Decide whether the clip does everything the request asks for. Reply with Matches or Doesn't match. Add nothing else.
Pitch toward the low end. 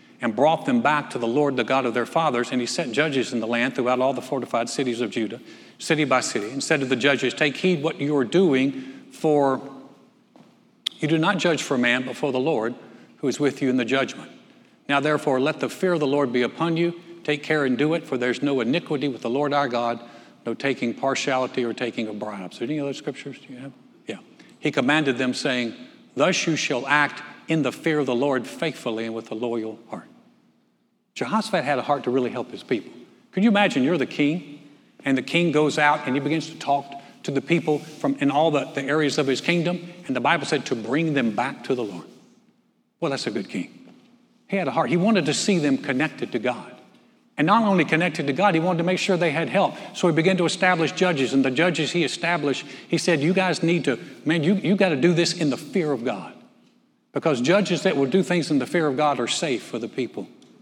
Doesn't match